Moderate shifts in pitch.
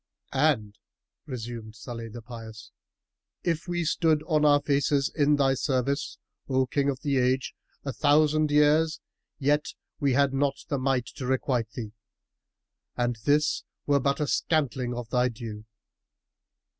Yes: average, 3.3 semitones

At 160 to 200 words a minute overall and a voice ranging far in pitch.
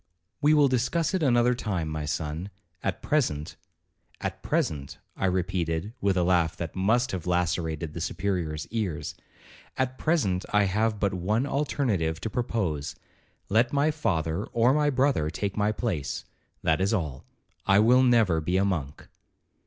No: average, 145 wpm; wide, 6.6 semitones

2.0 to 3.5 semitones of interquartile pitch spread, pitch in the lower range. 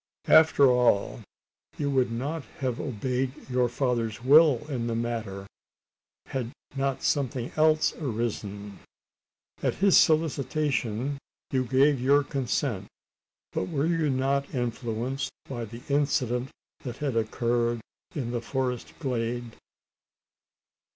Yes: average, 3.0 semitones; low, 125 Hz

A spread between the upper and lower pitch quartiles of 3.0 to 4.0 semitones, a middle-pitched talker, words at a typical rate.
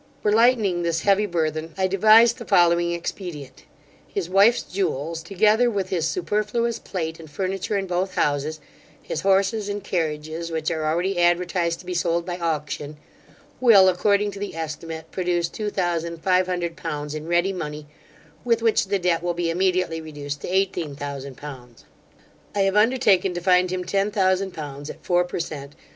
Yes: average, 3.4 semitones; medium, 175 Hz; average, 175 wpm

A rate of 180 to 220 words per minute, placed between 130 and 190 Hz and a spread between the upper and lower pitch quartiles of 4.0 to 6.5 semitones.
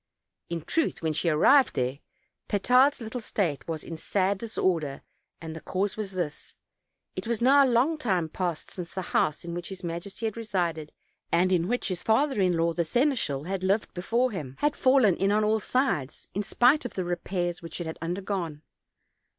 Yes: average, 190 wpm; medium, 185 Hz; wide, 5.4 semitones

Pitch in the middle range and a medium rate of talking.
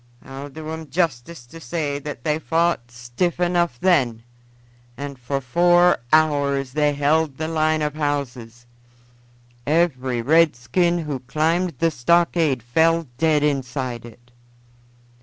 No: medium, 150 Hz; slow, 125 wpm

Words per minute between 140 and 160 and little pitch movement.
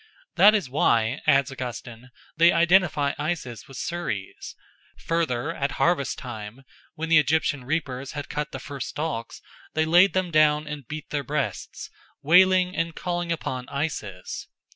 No: average, 145 wpm; average, 4.3 semitones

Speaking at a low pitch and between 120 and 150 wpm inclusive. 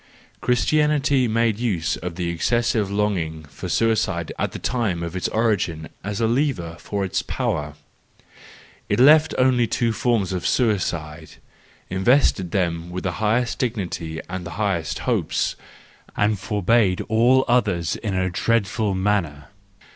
Yes: low, 105 Hz; average, 140 wpm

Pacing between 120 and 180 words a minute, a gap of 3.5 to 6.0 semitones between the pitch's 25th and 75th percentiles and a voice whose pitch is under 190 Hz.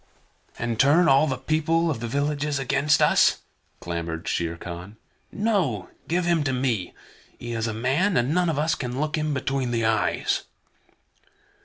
Yes: average, 165 wpm; average, 5.2 semitones; low, 135 Hz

